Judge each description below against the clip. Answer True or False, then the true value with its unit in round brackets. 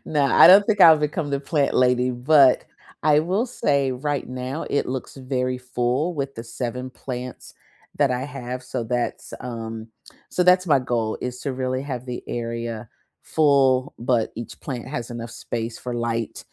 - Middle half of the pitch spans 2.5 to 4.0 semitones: True (2.8 semitones)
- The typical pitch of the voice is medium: False (130 Hz)